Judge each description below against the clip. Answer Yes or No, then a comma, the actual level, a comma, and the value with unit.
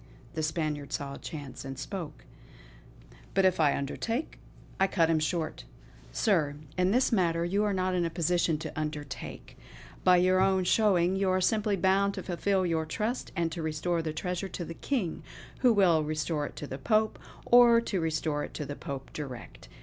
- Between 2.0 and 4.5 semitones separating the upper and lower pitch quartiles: Yes, average, 3.9 semitones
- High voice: No, medium, 175 Hz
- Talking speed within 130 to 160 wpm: No, average, 190 wpm